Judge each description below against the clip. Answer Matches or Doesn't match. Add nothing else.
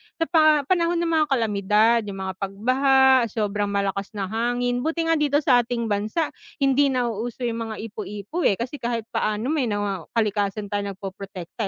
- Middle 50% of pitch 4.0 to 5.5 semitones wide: Matches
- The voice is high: Matches